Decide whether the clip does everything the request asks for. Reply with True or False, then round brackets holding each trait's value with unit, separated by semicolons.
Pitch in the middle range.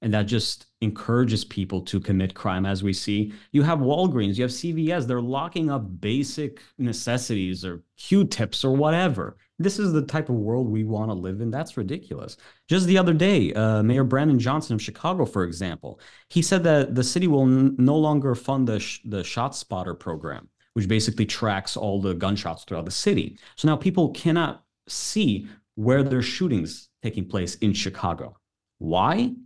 False (120 Hz)